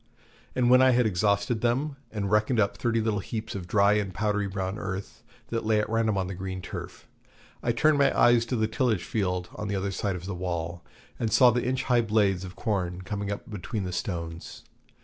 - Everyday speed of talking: No, fast, 215 wpm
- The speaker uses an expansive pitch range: No, average, 3.3 semitones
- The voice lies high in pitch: No, low, 105 Hz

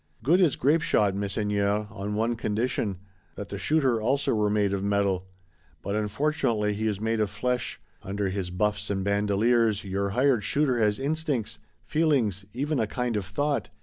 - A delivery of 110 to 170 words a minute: Yes, average, 165 wpm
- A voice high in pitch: No, low, 105 Hz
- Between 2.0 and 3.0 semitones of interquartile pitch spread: No, average, 3.8 semitones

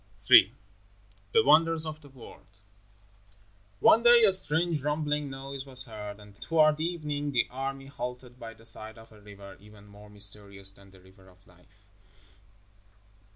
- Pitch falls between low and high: No, low, 125 Hz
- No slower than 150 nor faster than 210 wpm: Yes, average, 155 wpm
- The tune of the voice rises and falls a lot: Yes, wide, 6.4 semitones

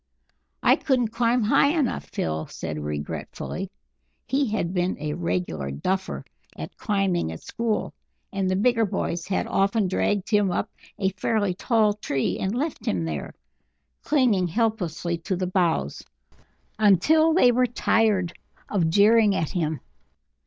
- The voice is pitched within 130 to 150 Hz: No, high, 195 Hz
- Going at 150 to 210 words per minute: No, average, 140 wpm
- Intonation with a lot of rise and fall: No, average, 4.9 semitones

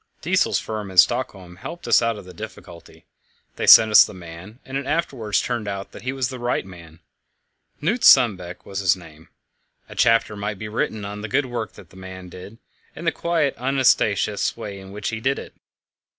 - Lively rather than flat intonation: No, average, 4.7 semitones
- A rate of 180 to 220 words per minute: Yes, average, 195 wpm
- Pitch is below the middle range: Yes, low, 105 Hz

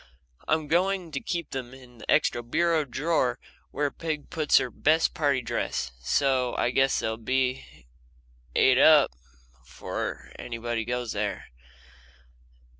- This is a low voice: Yes, low, 130 Hz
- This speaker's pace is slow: Yes, slow, 130 wpm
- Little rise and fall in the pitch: No, average, 4.4 semitones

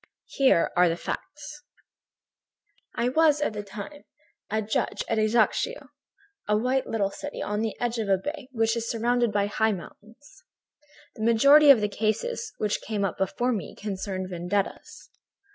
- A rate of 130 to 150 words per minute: No, average, 160 wpm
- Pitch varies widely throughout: No, average, 4.1 semitones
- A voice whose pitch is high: Yes, high, 220 Hz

